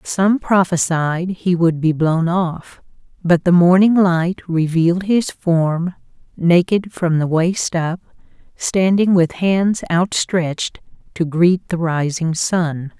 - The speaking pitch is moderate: Yes, medium, 175 Hz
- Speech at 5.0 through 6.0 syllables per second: No, 3.4 syllables/s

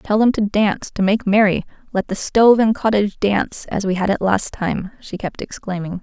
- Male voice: No, female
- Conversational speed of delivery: No, fast, 220 wpm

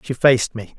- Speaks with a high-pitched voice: No, low, 120 Hz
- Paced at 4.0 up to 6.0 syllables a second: Yes, 5.9 syllables/s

